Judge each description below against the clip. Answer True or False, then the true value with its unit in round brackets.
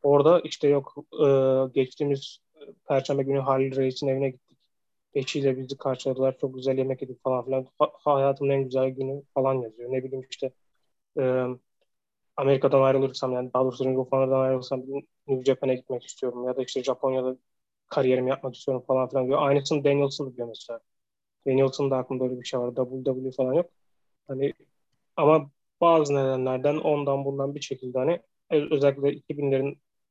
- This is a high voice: False (135 Hz)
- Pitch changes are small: True (1.3 semitones)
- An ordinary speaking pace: False (150 wpm)